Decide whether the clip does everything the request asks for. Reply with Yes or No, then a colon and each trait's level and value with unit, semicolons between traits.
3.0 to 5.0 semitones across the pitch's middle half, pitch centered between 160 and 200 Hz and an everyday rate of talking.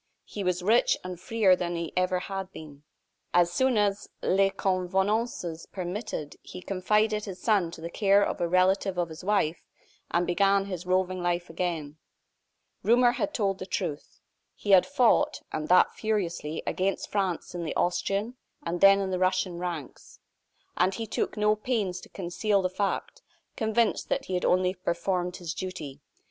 No: narrow, 2.5 semitones; medium, 185 Hz; average, 170 wpm